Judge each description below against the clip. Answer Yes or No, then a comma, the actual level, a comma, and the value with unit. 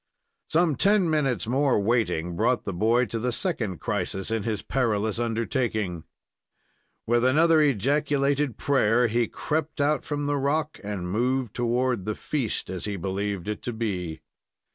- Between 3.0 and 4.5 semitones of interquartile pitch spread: No, average, 5.3 semitones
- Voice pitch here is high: No, low, 120 Hz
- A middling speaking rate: Yes, average, 150 wpm